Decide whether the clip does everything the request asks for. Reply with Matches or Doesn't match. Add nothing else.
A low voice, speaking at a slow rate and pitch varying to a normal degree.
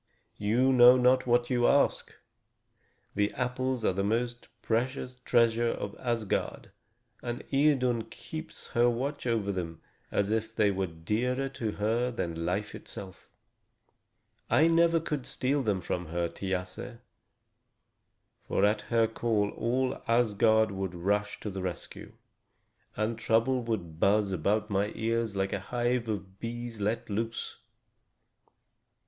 Matches